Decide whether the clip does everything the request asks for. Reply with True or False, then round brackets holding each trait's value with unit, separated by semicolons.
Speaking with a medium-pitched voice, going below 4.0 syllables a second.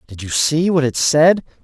False (145 Hz; 4.5 syllables/s)